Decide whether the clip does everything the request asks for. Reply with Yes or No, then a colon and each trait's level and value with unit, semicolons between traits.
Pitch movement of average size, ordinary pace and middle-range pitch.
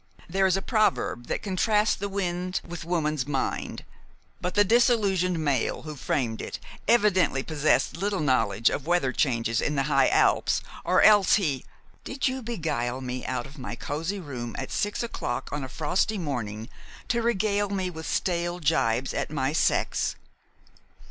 No: wide, 6.8 semitones; average, 165 wpm; medium, 165 Hz